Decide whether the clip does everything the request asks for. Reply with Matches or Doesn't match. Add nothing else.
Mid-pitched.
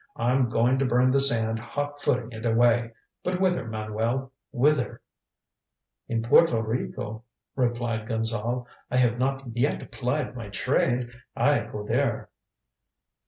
Doesn't match